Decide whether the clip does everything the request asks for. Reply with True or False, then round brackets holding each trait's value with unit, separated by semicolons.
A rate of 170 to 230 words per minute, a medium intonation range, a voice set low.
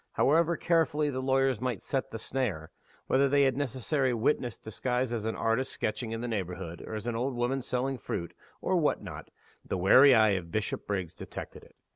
True (195 wpm; 3.6 semitones; 125 Hz)